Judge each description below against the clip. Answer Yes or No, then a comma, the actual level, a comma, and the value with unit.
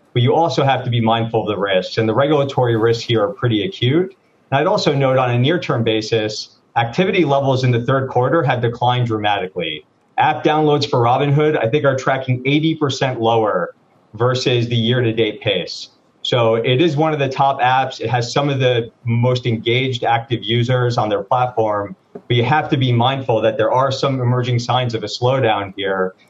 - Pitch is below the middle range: Yes, low, 125 Hz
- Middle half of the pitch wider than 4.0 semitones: No, average, 3.2 semitones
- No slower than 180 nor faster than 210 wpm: Yes, average, 200 wpm